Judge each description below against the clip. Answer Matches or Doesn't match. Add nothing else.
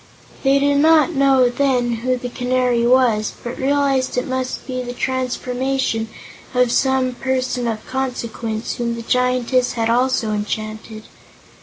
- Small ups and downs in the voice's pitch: Matches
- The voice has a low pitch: Doesn't match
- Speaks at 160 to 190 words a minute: Doesn't match